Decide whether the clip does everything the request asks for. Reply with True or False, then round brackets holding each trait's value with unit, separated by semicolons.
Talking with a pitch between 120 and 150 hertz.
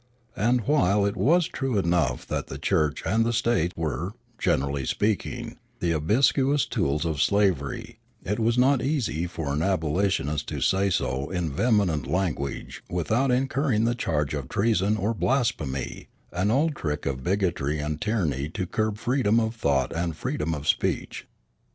False (95 Hz)